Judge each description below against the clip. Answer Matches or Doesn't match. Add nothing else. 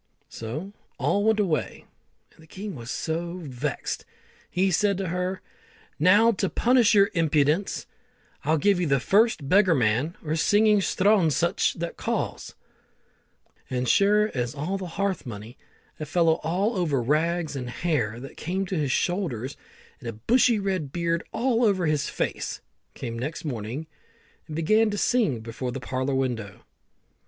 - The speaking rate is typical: Matches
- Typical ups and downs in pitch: Doesn't match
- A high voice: Doesn't match